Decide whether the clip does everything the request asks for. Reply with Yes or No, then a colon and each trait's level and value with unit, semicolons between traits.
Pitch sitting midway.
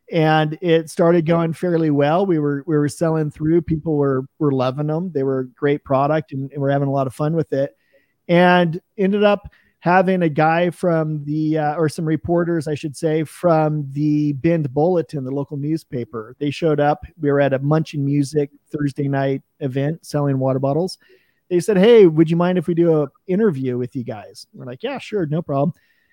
Yes: medium, 155 Hz